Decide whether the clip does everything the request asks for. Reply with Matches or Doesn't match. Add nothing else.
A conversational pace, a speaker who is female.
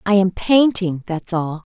Matches